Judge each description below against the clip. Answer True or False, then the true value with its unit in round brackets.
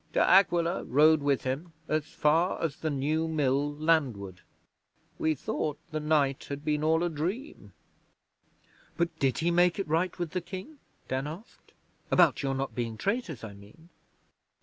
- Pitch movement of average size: True (3.6 semitones)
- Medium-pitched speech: True (155 Hz)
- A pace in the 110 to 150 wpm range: False (160 wpm)